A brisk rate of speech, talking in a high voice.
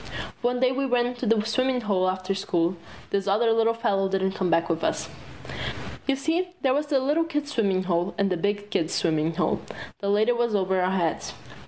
Yes: fast, 215 wpm; high, 205 Hz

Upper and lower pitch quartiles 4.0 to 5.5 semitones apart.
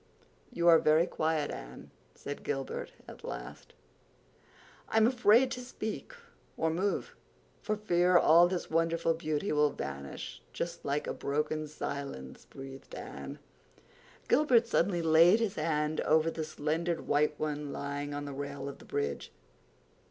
No: average, 3.3 semitones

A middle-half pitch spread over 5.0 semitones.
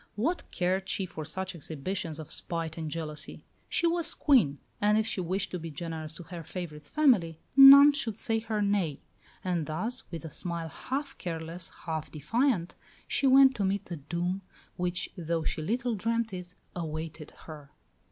Yes: wide, 5.5 semitones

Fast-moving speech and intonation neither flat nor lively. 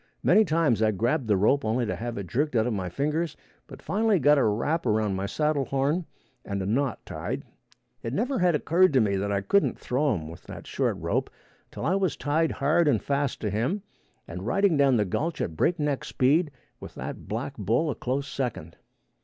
No: fast, 210 wpm; wide, 6.5 semitones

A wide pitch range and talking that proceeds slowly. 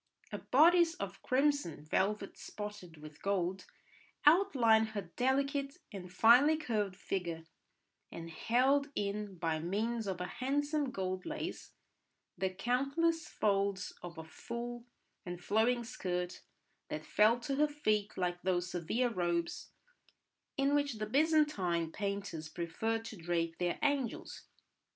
Yes: wide, 6.8 semitones; slow, 125 wpm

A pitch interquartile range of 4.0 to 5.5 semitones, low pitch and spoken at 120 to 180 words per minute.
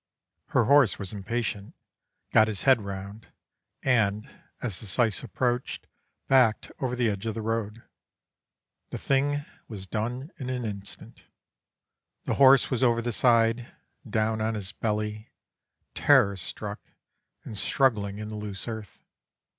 No: average, 2.9 semitones; low, 110 Hz; average, 140 wpm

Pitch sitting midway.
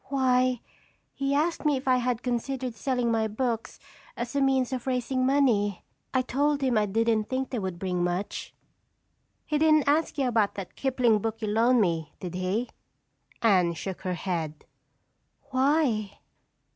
No: high, 240 Hz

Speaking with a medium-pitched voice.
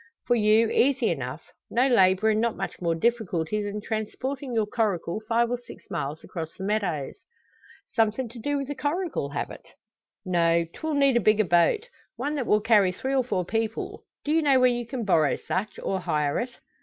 No: high, 220 Hz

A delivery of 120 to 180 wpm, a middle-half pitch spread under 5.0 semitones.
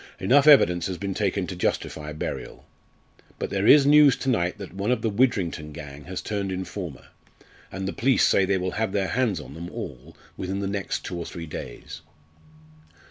No: average, 190 wpm; average, 3.5 semitones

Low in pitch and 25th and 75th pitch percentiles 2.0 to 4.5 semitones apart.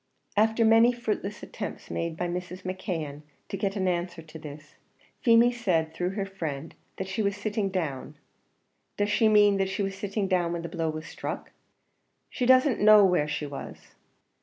No: high, 190 Hz; average, 4.0 semitones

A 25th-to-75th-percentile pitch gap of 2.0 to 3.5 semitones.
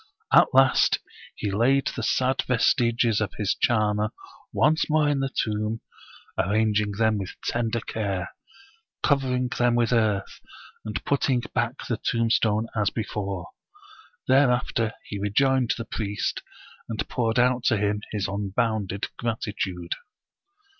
Yes: average, 3.0 semitones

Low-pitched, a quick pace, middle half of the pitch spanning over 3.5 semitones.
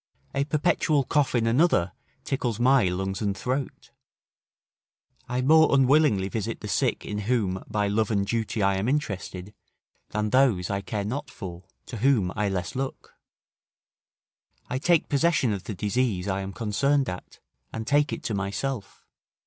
No: low, 110 Hz; average, 155 wpm; wide, 5.5 semitones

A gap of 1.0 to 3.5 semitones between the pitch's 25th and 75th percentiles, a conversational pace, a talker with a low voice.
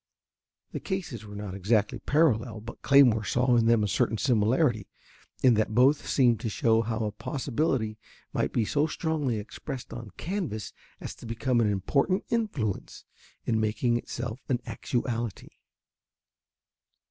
No: average, 4.0 semitones; average, 145 wpm; low, 120 Hz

